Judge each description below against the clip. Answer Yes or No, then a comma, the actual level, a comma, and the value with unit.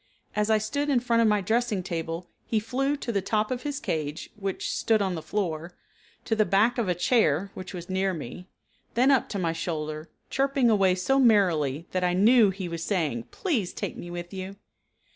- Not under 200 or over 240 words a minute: Yes, fast, 205 wpm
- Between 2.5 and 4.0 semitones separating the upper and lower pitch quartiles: No, average, 4.9 semitones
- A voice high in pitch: Yes, high, 195 Hz